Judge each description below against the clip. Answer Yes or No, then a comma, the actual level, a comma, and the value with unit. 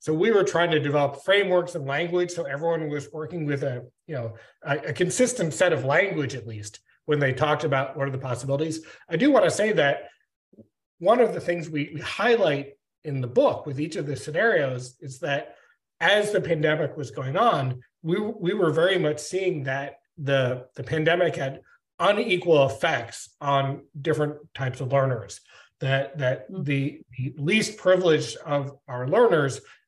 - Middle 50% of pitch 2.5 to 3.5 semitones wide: No, average, 4.0 semitones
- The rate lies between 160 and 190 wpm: Yes, average, 180 wpm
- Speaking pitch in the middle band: Yes, medium, 150 Hz